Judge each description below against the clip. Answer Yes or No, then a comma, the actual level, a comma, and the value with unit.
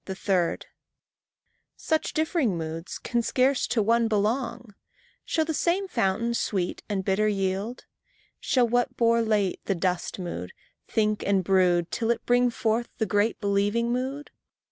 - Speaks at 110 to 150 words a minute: Yes, average, 145 wpm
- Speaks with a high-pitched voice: Yes, high, 220 Hz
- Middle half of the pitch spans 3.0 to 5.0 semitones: Yes, average, 4.0 semitones